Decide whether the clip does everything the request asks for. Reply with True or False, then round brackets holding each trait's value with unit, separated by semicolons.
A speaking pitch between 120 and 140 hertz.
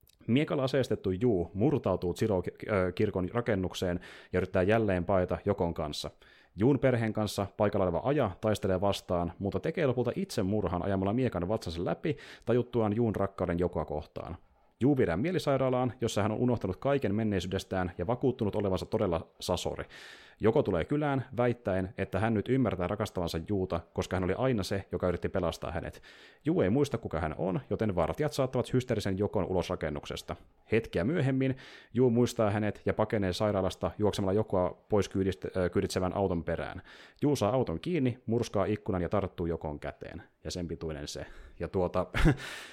False (100 Hz)